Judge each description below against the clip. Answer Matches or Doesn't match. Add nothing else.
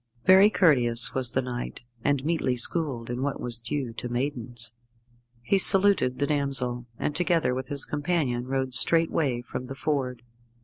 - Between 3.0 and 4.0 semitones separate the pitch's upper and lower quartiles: Matches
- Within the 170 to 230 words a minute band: Doesn't match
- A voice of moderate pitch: Doesn't match